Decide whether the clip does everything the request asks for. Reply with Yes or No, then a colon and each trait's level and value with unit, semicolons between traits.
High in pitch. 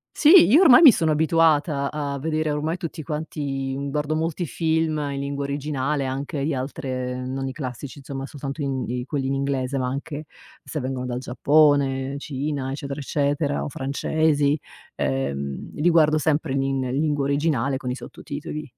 No: medium, 140 Hz